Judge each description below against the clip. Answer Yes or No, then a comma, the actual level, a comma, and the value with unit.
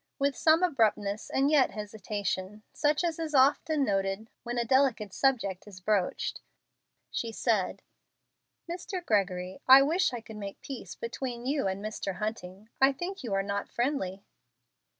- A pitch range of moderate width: No, wide, 5.7 semitones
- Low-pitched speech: No, high, 230 Hz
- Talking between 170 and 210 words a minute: No, average, 150 wpm